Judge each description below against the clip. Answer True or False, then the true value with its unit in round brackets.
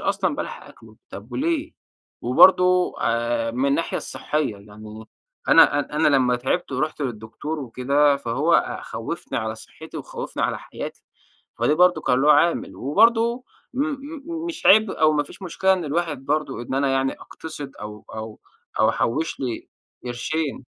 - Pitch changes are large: True (6.7 semitones)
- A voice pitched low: False (145 Hz)